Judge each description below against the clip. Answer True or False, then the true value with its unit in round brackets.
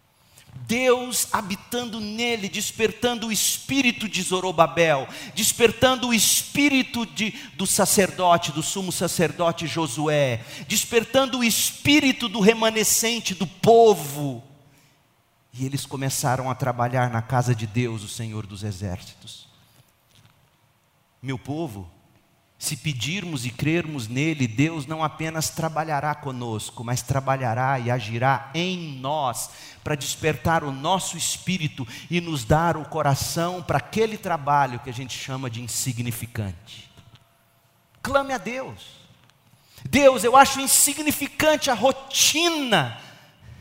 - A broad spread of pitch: True (8.7 semitones)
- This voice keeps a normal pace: False (115 wpm)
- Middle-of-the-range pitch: True (155 Hz)